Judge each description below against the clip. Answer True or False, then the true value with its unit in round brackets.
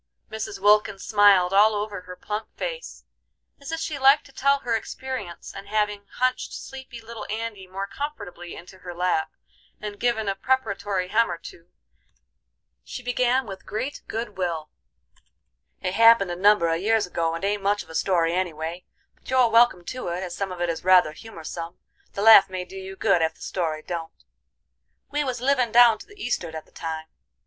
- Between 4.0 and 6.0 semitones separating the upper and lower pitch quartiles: True (4.5 semitones)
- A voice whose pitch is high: True (200 Hz)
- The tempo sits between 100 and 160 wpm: False (190 wpm)